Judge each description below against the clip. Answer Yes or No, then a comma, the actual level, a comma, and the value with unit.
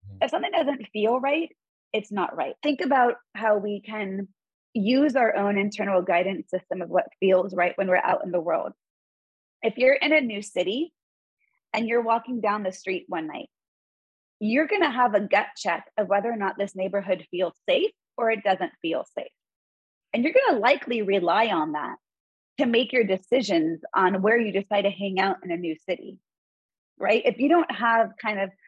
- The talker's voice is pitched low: No, high, 215 Hz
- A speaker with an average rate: Yes, average, 195 wpm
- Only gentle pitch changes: No, average, 5.2 semitones